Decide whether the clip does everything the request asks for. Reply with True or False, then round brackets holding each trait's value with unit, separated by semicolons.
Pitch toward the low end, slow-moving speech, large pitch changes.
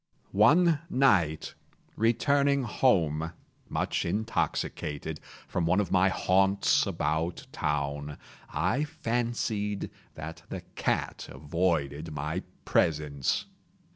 True (90 Hz; 90 wpm; 6.9 semitones)